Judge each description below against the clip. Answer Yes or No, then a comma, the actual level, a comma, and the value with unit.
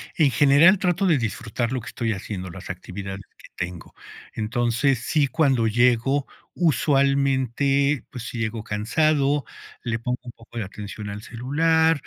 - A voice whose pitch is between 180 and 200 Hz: No, low, 125 Hz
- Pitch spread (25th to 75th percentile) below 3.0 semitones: No, average, 4.1 semitones